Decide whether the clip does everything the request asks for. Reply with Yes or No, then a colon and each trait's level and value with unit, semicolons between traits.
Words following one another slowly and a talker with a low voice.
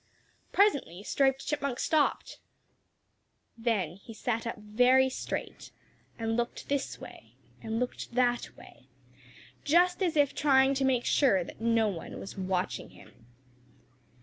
No: slow, 130 wpm; high, 245 Hz